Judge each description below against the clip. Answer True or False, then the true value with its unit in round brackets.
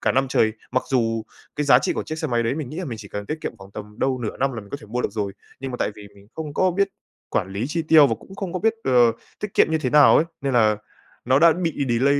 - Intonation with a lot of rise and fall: True (5.7 semitones)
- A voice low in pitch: True (130 Hz)